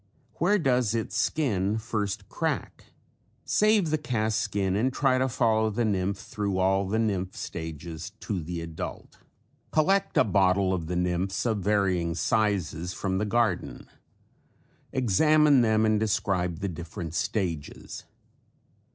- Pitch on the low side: Yes, low, 100 Hz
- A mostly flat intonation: No, average, 4.1 semitones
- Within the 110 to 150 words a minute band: Yes, slow, 135 wpm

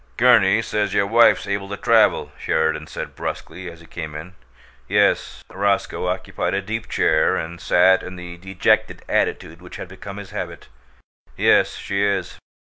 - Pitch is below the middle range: Yes, very low, 95 Hz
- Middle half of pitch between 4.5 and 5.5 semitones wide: No, average, 2.8 semitones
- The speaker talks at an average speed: Yes, average, 160 wpm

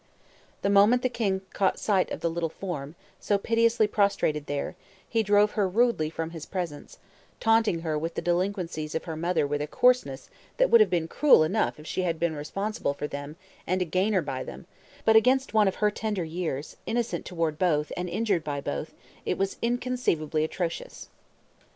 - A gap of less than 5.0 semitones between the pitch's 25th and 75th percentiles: No, wide, 5.4 semitones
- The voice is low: No, medium, 180 Hz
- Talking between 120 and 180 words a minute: No, average, 190 wpm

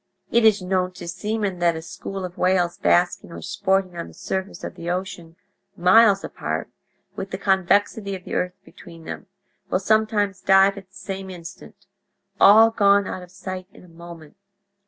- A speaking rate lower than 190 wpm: Yes, average, 175 wpm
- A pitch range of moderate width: No, narrow, 2.0 semitones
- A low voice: No, high, 190 Hz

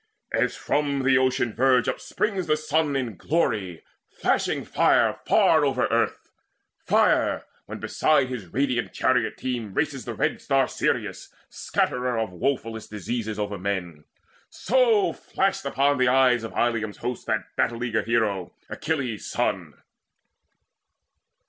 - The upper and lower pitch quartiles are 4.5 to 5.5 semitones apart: No, average, 4.0 semitones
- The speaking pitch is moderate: No, low, 125 Hz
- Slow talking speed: Yes, slow, 130 wpm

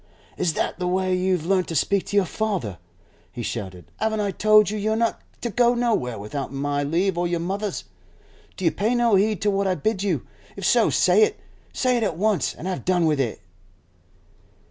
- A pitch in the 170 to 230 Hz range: Yes, high, 190 Hz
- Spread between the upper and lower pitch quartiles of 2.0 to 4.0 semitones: No, average, 4.6 semitones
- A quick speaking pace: Yes, fast, 210 wpm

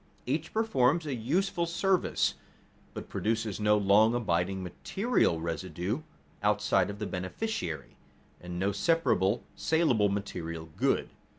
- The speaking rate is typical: No, slow, 115 wpm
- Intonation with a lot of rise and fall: Yes, wide, 9.0 semitones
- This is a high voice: No, low, 105 Hz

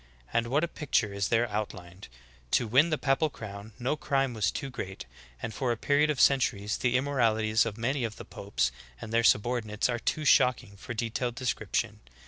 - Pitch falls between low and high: No, low, 120 Hz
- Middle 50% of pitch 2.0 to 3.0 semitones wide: No, average, 3.8 semitones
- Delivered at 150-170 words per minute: No, average, 200 wpm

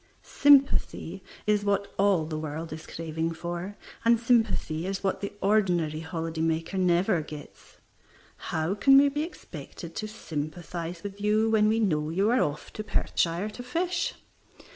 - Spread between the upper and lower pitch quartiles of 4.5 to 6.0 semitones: Yes, average, 4.8 semitones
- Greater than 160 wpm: No, average, 155 wpm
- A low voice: No, high, 190 Hz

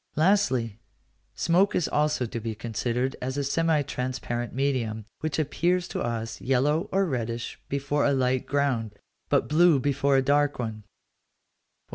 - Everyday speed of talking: Yes, average, 145 wpm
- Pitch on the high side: No, low, 135 Hz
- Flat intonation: No, average, 3.8 semitones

